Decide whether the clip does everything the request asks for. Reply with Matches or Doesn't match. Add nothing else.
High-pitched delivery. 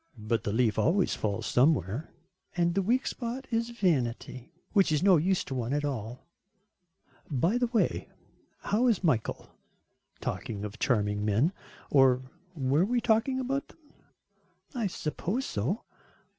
Doesn't match